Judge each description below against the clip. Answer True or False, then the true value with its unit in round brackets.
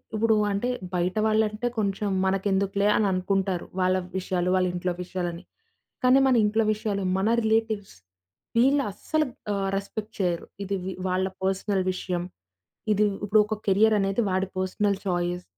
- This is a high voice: True (195 Hz)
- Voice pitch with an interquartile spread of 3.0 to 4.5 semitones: False (2.5 semitones)